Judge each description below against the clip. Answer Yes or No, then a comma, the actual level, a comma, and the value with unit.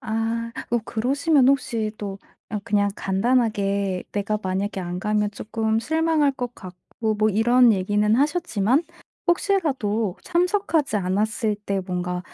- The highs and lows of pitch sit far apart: No, average, 4.5 semitones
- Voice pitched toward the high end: Yes, high, 220 Hz